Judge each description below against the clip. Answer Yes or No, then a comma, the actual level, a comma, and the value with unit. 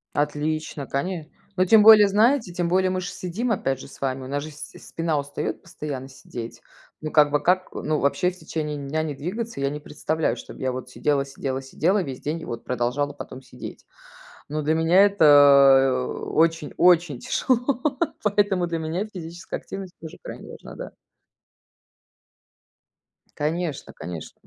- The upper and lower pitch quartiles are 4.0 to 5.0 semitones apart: Yes, average, 4.5 semitones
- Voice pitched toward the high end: No, medium, 155 Hz